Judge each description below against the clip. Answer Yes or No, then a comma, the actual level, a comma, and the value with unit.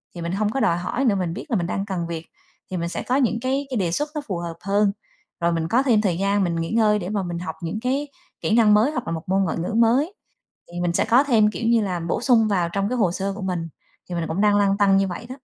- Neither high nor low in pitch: No, high, 200 Hz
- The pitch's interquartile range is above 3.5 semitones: Yes, average, 4.8 semitones